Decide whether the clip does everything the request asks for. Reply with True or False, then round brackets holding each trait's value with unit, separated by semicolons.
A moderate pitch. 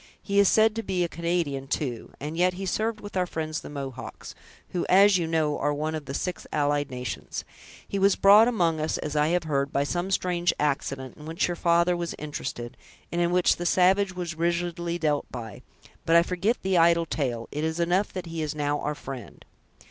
True (170 Hz)